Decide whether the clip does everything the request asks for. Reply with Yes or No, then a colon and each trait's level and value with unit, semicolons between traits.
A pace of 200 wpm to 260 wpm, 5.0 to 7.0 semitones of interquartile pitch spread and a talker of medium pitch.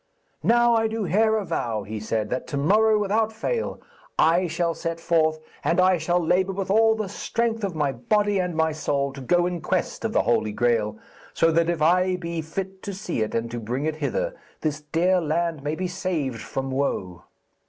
Yes: fast, 205 wpm; average, 5.3 semitones; medium, 170 Hz